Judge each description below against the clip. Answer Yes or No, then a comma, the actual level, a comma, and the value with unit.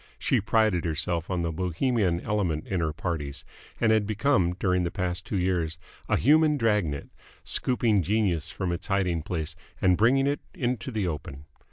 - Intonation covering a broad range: No, average, 4.5 semitones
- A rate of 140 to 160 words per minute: No, average, 175 wpm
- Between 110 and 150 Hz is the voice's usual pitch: No, very low, 90 Hz